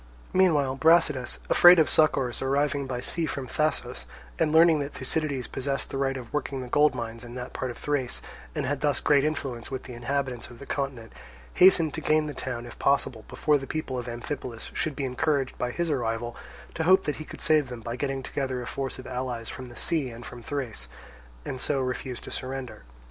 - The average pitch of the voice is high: No, low, 135 Hz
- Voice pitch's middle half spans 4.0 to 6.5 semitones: No, average, 3.1 semitones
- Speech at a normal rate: No, fast, 210 wpm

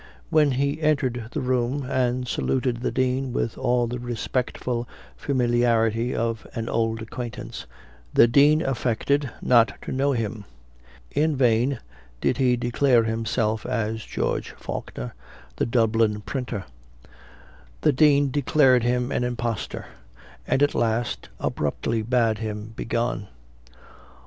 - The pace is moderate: No, slow, 125 wpm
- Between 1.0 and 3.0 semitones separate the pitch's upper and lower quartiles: Yes, narrow, 2.5 semitones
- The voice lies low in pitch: Yes, low, 120 Hz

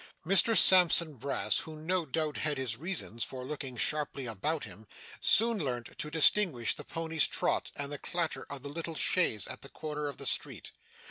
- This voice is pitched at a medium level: Yes, medium, 150 Hz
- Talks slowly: No, average, 185 wpm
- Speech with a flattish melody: No, average, 3.9 semitones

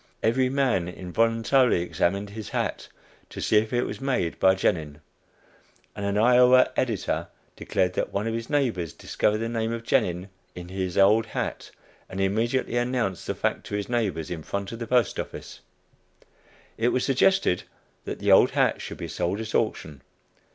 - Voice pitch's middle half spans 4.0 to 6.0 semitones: Yes, average, 4.4 semitones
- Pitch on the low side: Yes, low, 110 Hz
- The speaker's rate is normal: Yes, average, 170 wpm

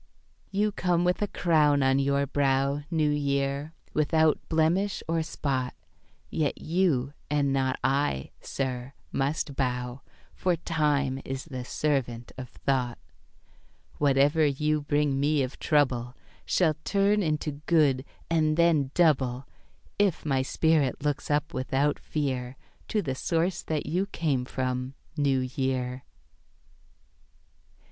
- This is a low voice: No, medium, 145 Hz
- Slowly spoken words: Yes, slow, 125 wpm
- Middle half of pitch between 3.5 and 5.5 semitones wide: No, average, 3.1 semitones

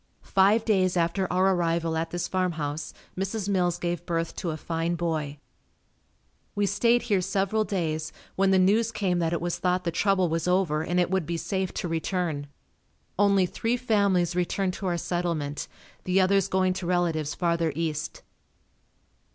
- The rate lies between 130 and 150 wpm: No, average, 170 wpm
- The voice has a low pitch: No, medium, 180 Hz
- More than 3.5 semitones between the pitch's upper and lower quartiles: No, narrow, 2.6 semitones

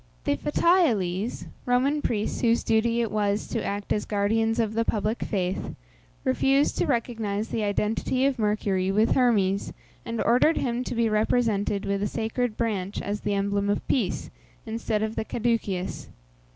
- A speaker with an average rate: Yes, average, 160 wpm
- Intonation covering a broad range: No, average, 2.8 semitones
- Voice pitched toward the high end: Yes, high, 220 Hz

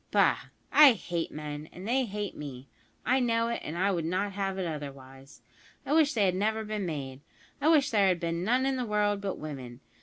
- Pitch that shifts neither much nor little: No, wide, 6.8 semitones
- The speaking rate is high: Yes, fast, 215 wpm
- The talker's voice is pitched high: Yes, high, 195 Hz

